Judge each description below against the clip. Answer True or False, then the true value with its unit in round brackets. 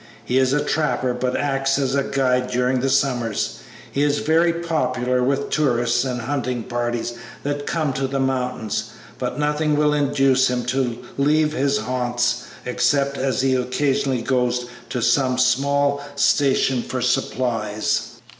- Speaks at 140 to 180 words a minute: True (145 wpm)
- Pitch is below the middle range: True (130 Hz)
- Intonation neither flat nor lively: False (2.2 semitones)